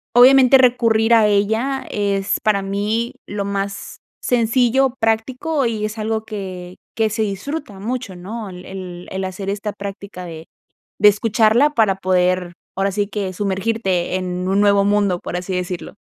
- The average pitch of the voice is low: No, high, 205 Hz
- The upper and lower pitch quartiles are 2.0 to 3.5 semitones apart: Yes, average, 2.9 semitones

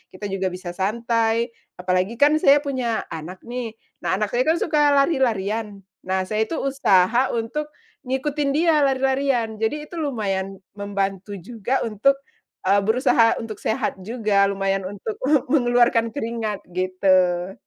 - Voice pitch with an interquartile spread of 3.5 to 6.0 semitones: Yes, average, 5.3 semitones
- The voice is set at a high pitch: Yes, high, 225 Hz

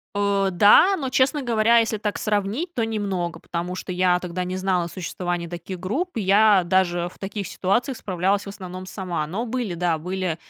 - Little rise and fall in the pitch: No, average, 3.4 semitones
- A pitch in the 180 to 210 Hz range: Yes, high, 190 Hz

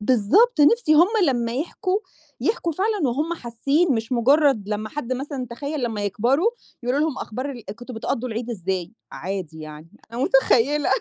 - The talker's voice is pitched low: No, very high, 255 Hz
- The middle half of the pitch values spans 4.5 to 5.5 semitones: Yes, average, 5.0 semitones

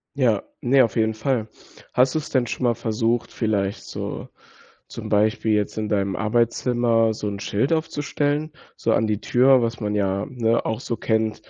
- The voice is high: No, low, 115 Hz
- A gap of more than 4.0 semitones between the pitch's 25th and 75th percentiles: No, average, 2.7 semitones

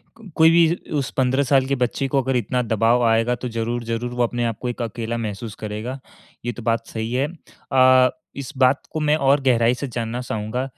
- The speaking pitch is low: Yes, low, 125 Hz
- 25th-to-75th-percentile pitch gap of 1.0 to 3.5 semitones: Yes, narrow, 2.5 semitones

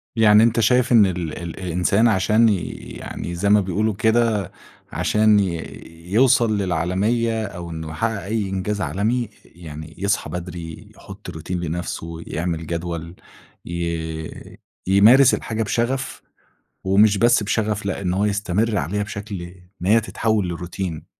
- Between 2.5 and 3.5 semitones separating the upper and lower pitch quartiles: No, average, 4.1 semitones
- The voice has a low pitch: Yes, low, 100 Hz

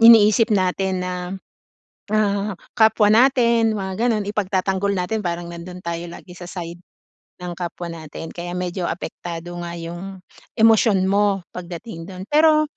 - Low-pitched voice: No, high, 190 Hz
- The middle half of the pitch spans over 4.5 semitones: No, average, 3.6 semitones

